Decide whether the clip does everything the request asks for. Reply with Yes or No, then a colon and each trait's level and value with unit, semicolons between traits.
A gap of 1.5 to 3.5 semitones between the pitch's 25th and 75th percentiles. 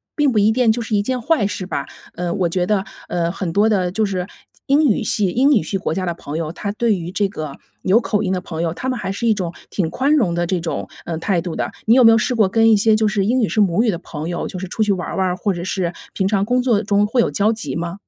No: average, 4.0 semitones